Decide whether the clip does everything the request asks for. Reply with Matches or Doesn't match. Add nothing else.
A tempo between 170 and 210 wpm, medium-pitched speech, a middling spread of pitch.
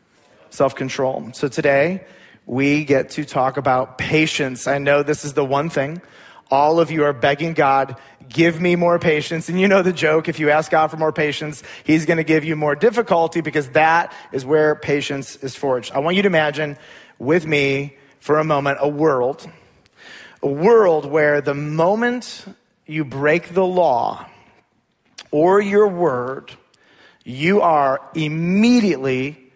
Doesn't match